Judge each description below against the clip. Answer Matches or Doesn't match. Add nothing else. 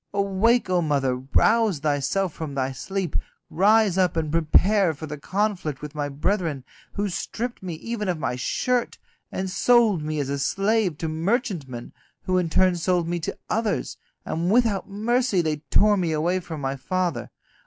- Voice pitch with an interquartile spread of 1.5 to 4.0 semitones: Doesn't match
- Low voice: Doesn't match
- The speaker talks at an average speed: Matches